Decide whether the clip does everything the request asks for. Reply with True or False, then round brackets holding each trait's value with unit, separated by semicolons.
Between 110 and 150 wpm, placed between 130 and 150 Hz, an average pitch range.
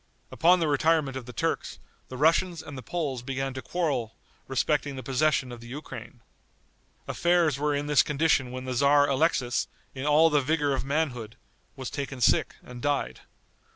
False (175 wpm; 140 Hz; 3.1 semitones)